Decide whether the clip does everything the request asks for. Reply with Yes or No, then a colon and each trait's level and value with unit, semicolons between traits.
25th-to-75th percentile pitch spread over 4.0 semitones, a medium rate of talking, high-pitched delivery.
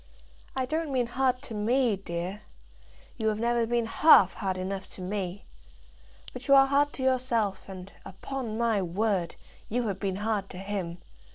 Yes: average, 4.7 semitones; average, 170 wpm; high, 215 Hz